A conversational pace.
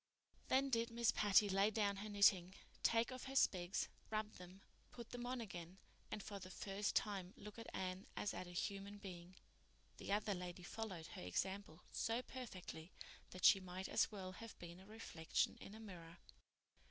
Yes: average, 180 wpm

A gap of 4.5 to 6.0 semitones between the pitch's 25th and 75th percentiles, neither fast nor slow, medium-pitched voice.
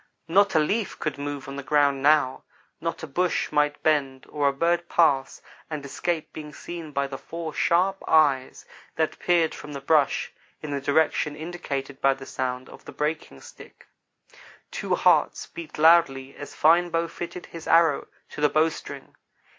No: average, 3.1 semitones; average, 170 wpm; medium, 150 Hz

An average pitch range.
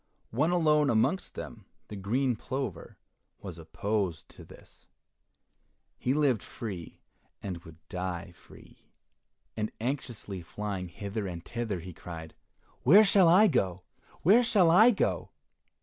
No: wide, 8.5 semitones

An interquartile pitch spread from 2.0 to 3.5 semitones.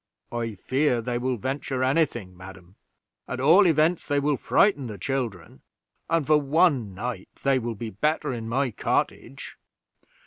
No: average, 4.5 semitones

